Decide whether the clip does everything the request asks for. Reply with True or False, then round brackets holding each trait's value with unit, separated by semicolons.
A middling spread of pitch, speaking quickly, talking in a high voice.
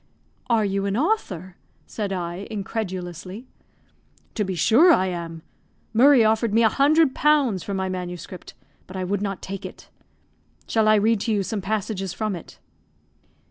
False (3.3 semitones; 155 wpm; 200 Hz)